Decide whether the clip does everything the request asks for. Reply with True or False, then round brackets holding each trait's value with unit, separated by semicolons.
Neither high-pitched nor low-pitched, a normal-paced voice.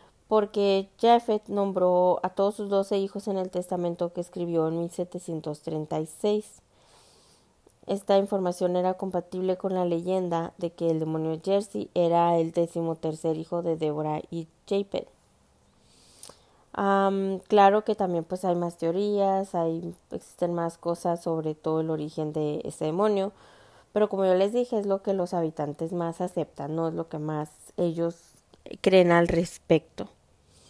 True (175 Hz; 150 wpm)